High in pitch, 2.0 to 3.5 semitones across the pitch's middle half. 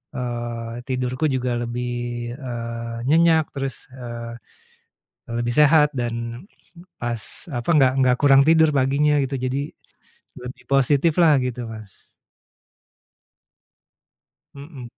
No: low, 125 Hz; average, 3.0 semitones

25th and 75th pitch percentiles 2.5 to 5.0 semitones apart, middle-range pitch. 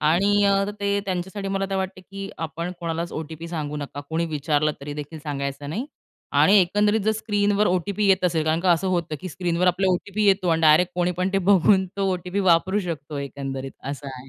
Yes: average, 4.0 semitones; medium, 175 Hz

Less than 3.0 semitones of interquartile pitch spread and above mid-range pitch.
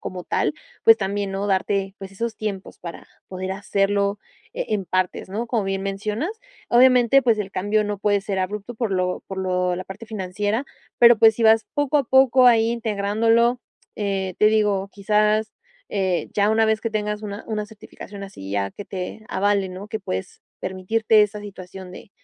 Yes: narrow, 2.4 semitones; high, 205 Hz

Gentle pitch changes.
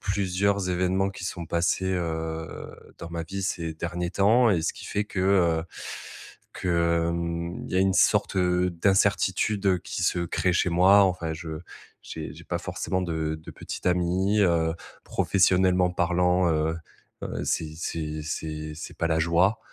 Yes: narrow, 2.2 semitones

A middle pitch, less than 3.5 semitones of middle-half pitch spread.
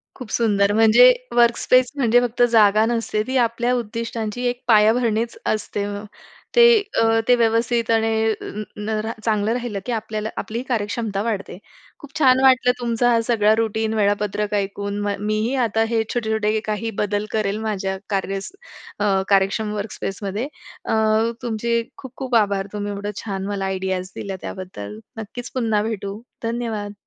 No: high, 220 Hz; narrow, 2.4 semitones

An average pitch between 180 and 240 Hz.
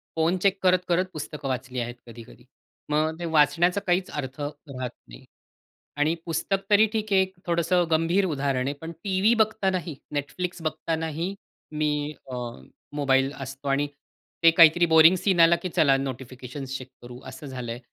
No: medium, 155 Hz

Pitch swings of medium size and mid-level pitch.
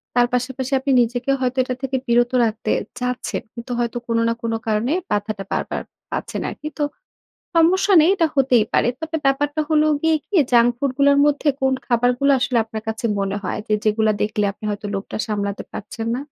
No: average, 4.0 semitones; high, 245 Hz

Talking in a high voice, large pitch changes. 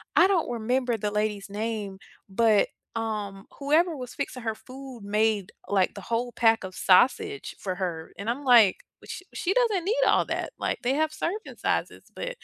Yes: high, 230 Hz; wide, 5.8 semitones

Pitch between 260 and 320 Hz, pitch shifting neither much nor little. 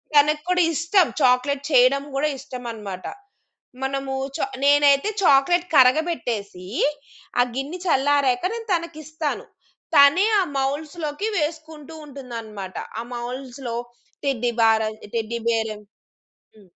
Yes: very high, 275 Hz; average, 4.1 semitones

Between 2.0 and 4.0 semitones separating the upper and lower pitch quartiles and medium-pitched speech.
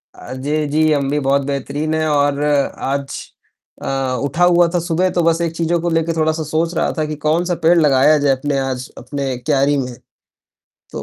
Yes: average, 2.9 semitones; medium, 150 Hz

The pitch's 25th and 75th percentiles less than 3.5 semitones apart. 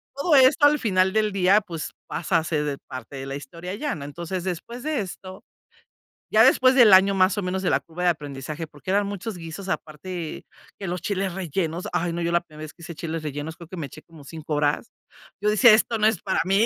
No: average, 4.1 semitones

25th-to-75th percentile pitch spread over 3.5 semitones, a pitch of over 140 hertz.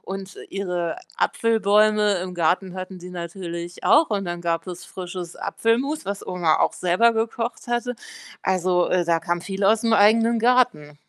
Yes: average, 4.2 semitones; high, 190 Hz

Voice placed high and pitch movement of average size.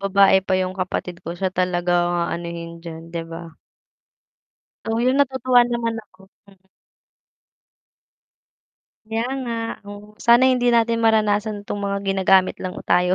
Yes: high, 200 Hz; average, 4.0 semitones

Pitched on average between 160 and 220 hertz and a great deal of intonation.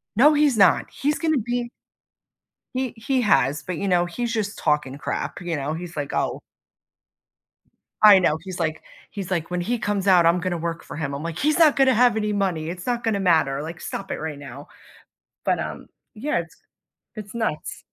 Yes: medium, 185 Hz; wide, 6.5 semitones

